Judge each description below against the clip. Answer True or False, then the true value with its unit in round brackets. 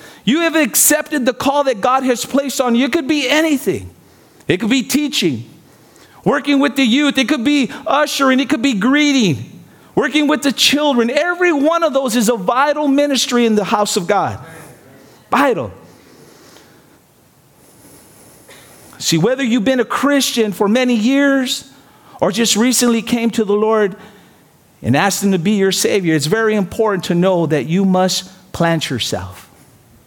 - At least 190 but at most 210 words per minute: False (165 wpm)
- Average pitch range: False (6.9 semitones)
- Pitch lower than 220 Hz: False (240 Hz)